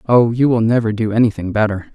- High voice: No, low, 110 Hz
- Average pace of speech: No, fast, 215 wpm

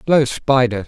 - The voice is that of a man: Yes, male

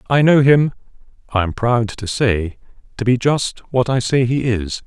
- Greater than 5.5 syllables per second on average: No, 4.4 syllables/s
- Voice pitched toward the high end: No, low, 120 Hz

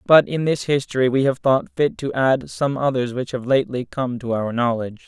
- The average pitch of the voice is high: No, low, 130 Hz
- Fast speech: Yes, fast, 225 wpm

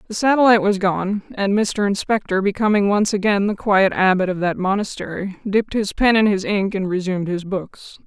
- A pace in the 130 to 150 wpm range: No, average, 195 wpm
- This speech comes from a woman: Yes, female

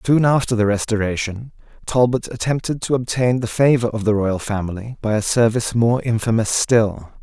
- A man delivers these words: Yes, male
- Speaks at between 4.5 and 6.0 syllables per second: Yes, 5.3 syllables/s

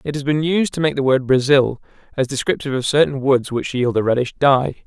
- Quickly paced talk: Yes, fast, 235 wpm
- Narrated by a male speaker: Yes, male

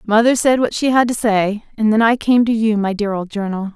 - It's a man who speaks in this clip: No, female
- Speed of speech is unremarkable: No, fast, 270 wpm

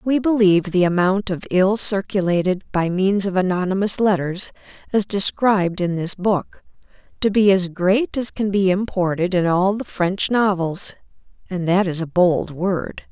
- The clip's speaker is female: Yes, female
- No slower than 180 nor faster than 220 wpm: No, average, 165 wpm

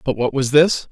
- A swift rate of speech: Yes, fast, 265 wpm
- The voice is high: No, medium, 140 Hz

